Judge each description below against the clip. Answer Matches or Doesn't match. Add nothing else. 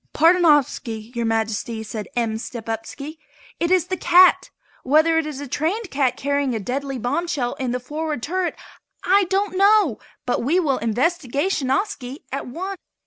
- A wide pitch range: Matches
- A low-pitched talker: Doesn't match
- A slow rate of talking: Doesn't match